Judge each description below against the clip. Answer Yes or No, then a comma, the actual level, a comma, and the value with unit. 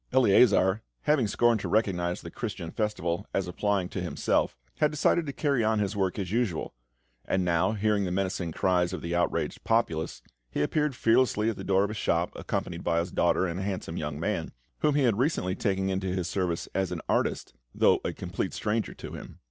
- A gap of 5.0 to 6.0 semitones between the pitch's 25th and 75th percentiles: No, average, 4.0 semitones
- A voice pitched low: Yes, very low, 95 Hz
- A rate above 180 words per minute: Yes, fast, 205 wpm